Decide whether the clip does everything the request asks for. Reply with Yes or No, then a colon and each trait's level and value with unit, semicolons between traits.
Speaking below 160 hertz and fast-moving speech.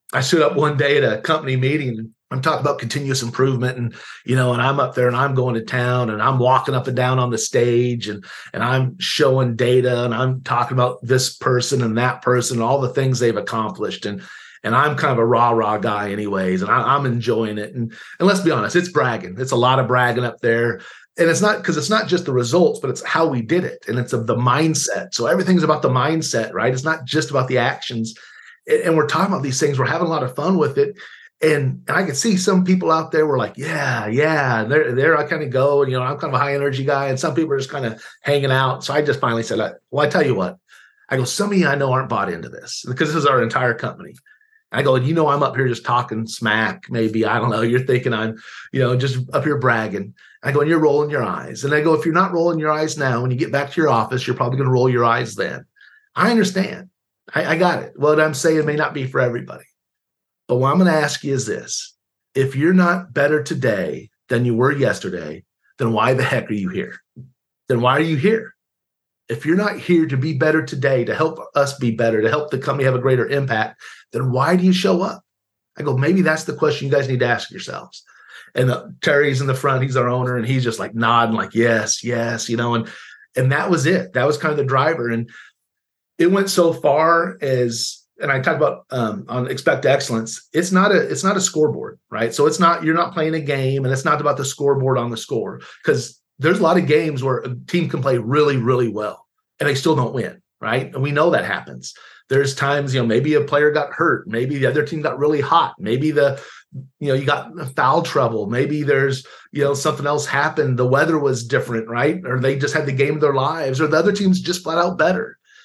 Yes: medium, 140 Hz; fast, 250 wpm